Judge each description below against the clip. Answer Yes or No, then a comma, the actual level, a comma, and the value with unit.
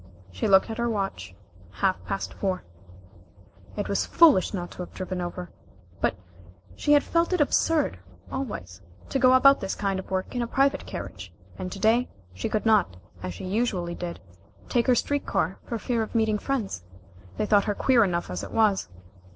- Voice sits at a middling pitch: No, high, 205 Hz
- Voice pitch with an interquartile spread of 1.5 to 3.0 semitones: No, average, 5.1 semitones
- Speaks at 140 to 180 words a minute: No, average, 190 wpm